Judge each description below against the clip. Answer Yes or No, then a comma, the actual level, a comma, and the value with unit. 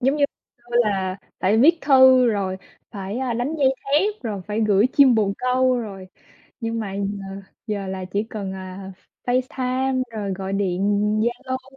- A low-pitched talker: No, high, 225 Hz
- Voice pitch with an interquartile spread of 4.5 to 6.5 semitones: Yes, average, 4.8 semitones